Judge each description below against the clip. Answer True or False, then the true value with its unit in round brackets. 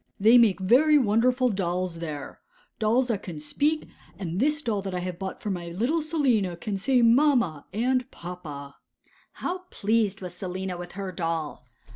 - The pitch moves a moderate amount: False (5.9 semitones)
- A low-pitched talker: False (200 Hz)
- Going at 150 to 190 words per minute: True (160 wpm)